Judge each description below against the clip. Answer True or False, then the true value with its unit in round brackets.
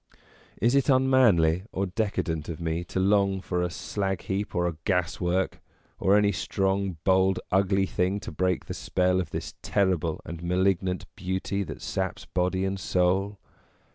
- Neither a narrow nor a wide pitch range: False (1.8 semitones)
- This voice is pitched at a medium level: False (95 Hz)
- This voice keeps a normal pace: True (160 wpm)